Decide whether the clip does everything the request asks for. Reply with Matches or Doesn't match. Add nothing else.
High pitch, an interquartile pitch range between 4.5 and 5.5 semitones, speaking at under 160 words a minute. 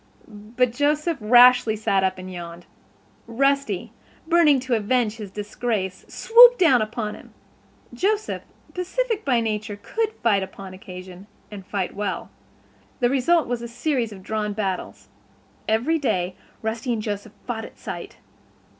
Matches